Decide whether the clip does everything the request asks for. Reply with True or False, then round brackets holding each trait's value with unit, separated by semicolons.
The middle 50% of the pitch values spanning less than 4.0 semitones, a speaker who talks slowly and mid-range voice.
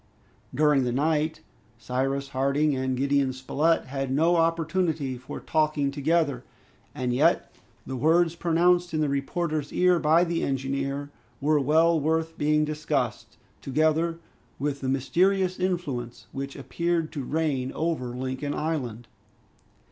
True (3.3 semitones; 130 wpm; 150 Hz)